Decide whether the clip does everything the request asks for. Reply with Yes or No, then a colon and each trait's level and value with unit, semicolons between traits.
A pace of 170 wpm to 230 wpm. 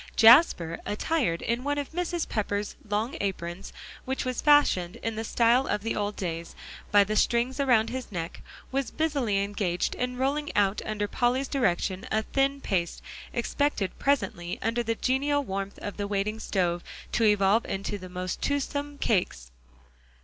No: average, 155 wpm